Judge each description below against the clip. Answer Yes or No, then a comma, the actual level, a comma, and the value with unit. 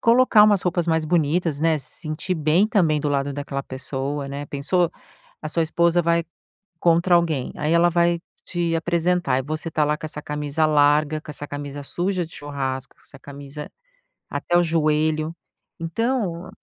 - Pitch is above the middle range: No, medium, 155 Hz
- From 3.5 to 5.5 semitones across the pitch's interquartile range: No, average, 2.9 semitones